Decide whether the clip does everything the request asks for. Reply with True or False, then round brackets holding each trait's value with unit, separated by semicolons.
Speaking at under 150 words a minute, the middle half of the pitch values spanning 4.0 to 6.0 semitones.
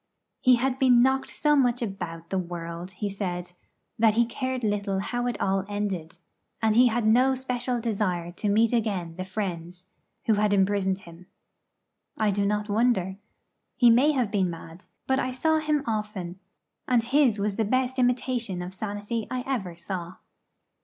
False (170 wpm; 4.6 semitones)